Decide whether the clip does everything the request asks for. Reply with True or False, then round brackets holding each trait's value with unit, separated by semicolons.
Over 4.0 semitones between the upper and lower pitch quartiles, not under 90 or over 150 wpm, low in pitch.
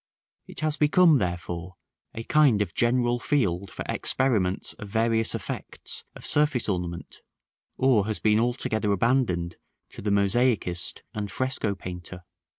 True (5.5 semitones; 135 wpm; 110 Hz)